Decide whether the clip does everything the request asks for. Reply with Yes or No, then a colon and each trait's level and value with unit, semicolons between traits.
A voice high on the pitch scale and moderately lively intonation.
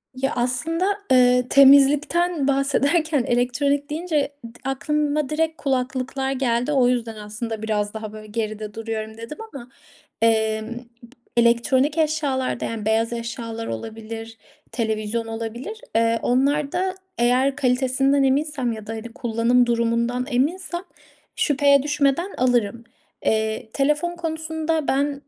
Yes: very high, 250 Hz; average, 3.9 semitones